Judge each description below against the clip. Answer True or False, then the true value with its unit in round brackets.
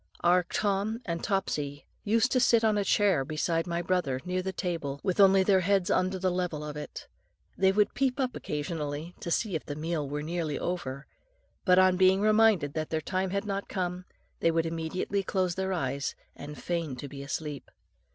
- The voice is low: False (180 Hz)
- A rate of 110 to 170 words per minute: False (195 wpm)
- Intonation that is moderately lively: True (4.1 semitones)